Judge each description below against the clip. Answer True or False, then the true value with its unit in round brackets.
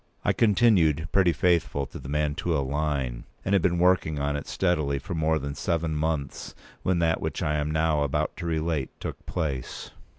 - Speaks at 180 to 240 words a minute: True (185 wpm)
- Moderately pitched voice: False (80 Hz)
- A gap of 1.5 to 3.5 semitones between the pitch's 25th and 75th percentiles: True (3.0 semitones)